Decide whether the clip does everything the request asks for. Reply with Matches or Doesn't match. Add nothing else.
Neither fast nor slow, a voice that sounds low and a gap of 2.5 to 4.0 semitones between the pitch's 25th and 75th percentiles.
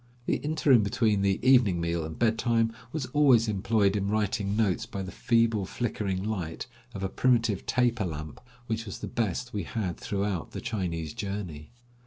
Matches